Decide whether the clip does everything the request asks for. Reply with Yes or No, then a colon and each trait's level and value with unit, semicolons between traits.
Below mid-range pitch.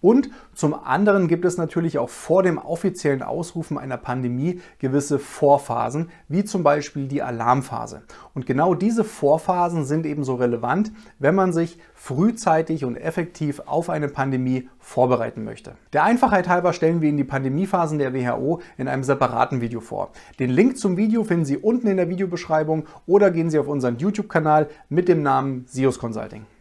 No: medium, 155 Hz